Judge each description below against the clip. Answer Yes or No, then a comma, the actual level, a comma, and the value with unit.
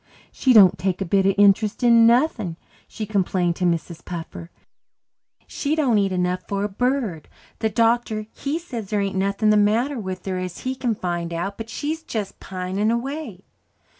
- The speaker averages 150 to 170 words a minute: No, average, 180 wpm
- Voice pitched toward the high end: Yes, high, 205 Hz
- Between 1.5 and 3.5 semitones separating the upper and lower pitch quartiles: No, average, 4.2 semitones